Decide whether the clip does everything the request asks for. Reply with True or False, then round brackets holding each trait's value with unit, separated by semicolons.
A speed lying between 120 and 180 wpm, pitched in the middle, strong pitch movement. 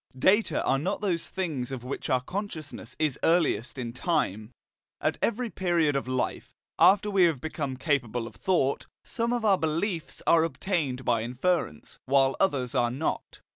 True (165 wpm; 155 Hz; 6.3 semitones)